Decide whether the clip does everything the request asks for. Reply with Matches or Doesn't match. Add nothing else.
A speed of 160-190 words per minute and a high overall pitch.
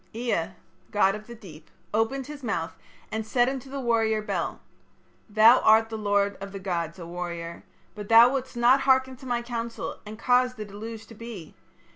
Matches